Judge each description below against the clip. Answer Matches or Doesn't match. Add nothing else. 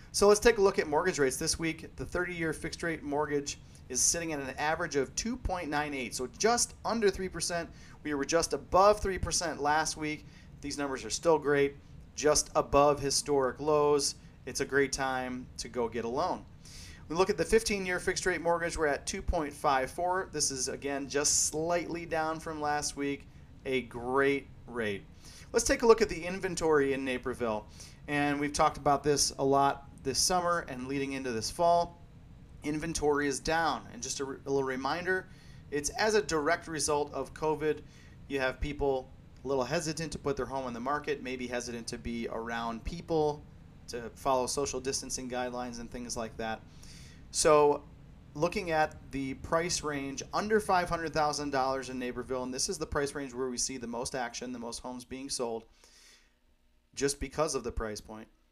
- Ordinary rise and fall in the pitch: Matches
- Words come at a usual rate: Matches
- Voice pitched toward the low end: Doesn't match